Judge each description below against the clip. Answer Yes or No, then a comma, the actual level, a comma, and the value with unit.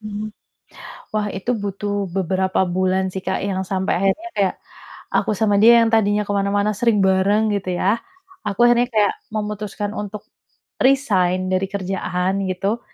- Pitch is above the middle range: Yes, high, 200 Hz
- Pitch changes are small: Yes, narrow, 2.0 semitones